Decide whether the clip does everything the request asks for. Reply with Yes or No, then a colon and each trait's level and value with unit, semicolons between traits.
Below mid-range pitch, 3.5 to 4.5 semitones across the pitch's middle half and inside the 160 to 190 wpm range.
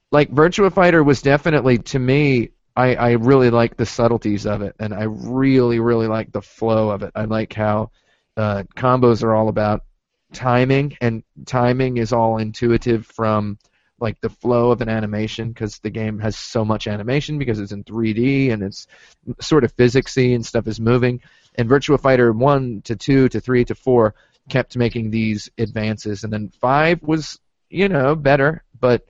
No: low, 120 Hz; average, 3.1 semitones; average, 180 wpm